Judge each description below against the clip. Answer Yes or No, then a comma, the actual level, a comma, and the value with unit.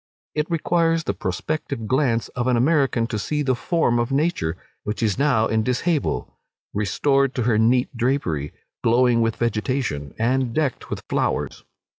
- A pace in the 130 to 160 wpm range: Yes, average, 155 wpm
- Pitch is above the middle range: No, low, 125 Hz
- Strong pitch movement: No, average, 3.9 semitones